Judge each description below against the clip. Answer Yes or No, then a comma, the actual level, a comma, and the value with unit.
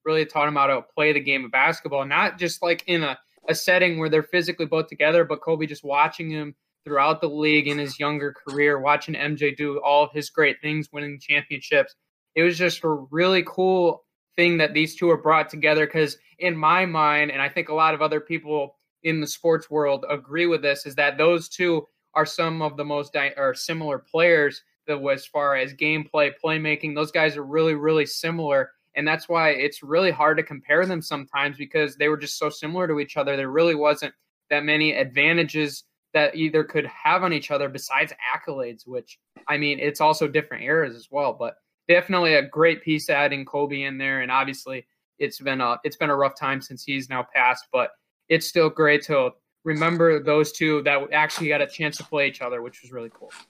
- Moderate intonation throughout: No, narrow, 1.9 semitones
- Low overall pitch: No, medium, 150 Hz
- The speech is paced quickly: Yes, fast, 210 wpm